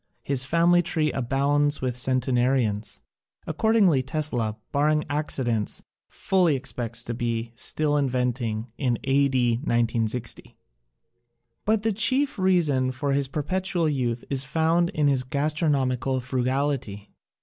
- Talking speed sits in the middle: No, slow, 125 wpm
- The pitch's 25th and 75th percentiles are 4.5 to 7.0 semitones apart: No, average, 3.9 semitones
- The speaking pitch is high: No, low, 135 Hz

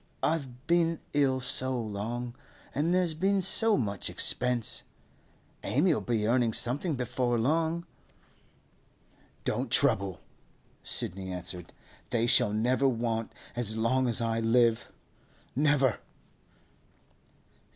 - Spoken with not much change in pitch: No, average, 4.4 semitones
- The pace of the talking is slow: Yes, slow, 100 wpm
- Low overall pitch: Yes, low, 125 Hz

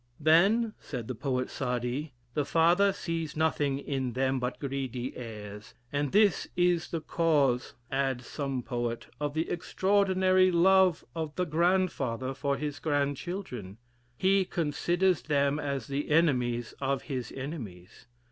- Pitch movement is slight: No, average, 4.9 semitones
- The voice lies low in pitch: No, medium, 145 Hz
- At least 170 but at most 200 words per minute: No, slow, 135 wpm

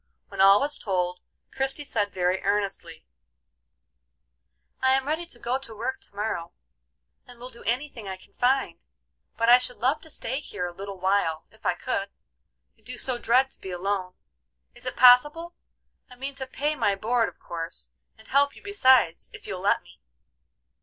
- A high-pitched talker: Yes, high, 235 Hz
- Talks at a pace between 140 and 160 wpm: No, average, 185 wpm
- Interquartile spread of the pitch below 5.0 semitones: No, wide, 5.4 semitones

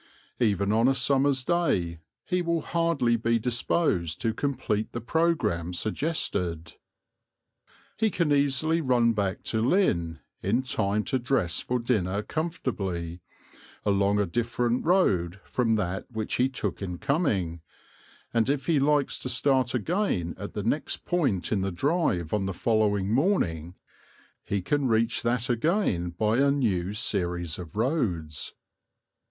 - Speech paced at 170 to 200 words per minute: No, average, 140 wpm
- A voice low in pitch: Yes, low, 115 Hz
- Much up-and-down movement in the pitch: Yes, wide, 6.6 semitones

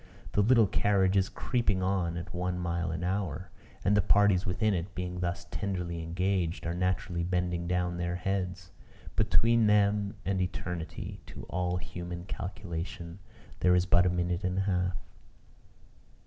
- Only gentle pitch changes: Yes, narrow, 2.0 semitones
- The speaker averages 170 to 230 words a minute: No, average, 155 wpm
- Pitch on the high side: No, very low, 90 Hz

